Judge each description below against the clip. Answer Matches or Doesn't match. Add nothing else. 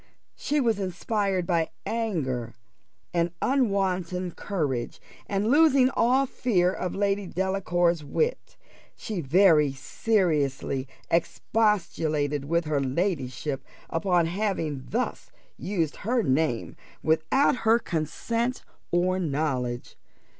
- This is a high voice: Doesn't match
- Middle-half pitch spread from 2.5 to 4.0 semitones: Doesn't match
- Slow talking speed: Matches